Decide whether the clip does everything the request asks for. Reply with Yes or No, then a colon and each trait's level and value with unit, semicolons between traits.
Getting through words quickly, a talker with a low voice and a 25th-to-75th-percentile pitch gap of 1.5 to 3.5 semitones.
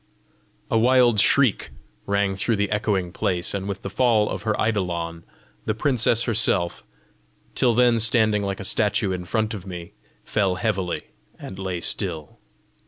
No: average, 155 wpm; low, 100 Hz; average, 3.1 semitones